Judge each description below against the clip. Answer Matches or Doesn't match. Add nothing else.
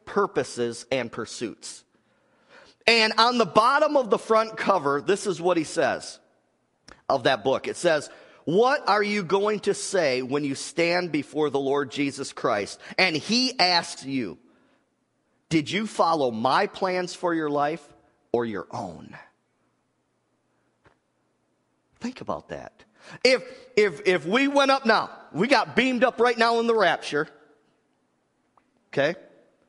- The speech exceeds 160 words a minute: Doesn't match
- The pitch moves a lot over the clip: Matches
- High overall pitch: Doesn't match